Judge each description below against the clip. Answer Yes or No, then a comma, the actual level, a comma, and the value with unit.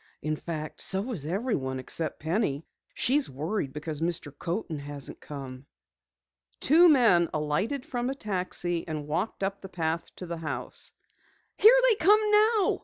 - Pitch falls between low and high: Yes, medium, 170 Hz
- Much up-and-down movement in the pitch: Yes, wide, 8.0 semitones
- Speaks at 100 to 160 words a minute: Yes, average, 150 wpm